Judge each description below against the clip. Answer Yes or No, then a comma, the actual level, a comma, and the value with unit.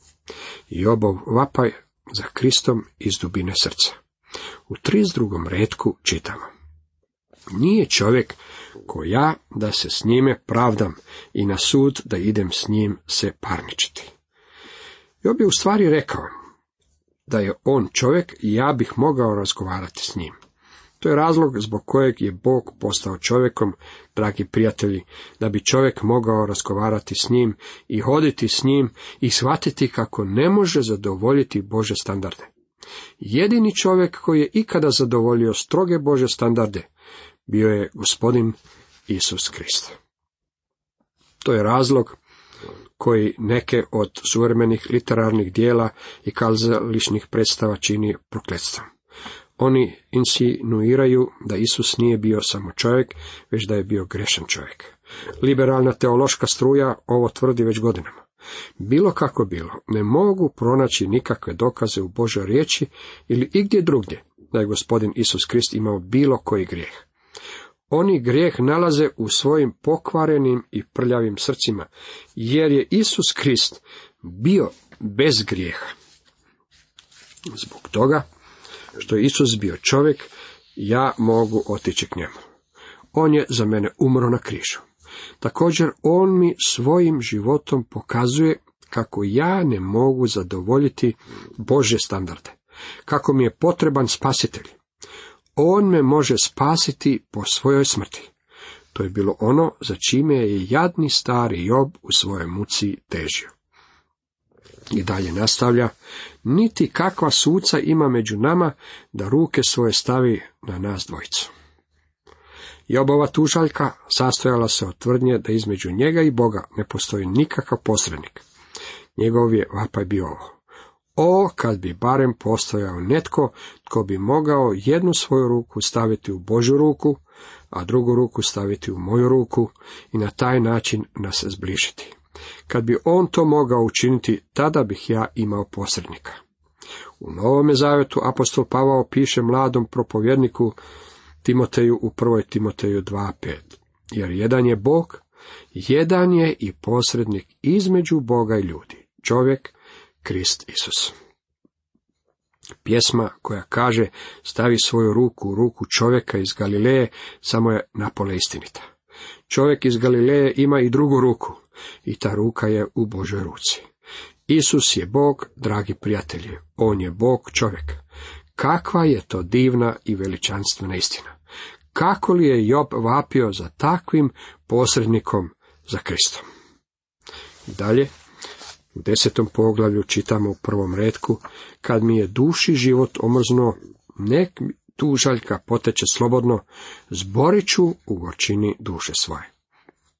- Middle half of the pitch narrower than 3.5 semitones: No, average, 4.6 semitones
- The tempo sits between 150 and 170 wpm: No, average, 125 wpm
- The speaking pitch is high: No, low, 115 Hz